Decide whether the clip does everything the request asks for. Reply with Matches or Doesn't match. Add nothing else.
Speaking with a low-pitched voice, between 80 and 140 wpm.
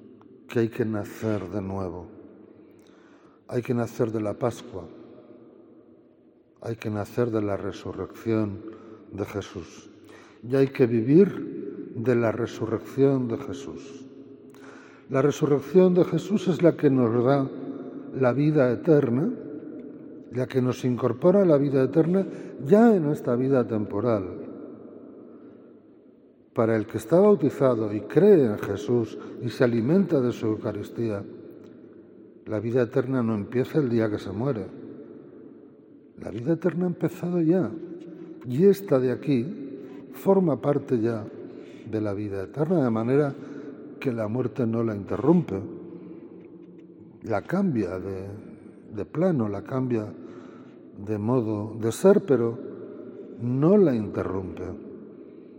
Matches